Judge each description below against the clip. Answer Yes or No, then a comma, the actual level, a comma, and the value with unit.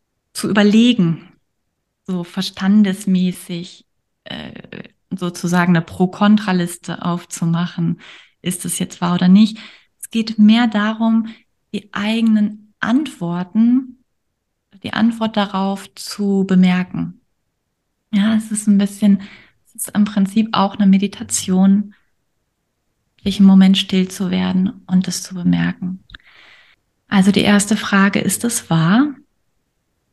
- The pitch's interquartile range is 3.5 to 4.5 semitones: No, average, 2.9 semitones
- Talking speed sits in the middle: No, slow, 110 wpm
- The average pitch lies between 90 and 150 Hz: No, high, 195 Hz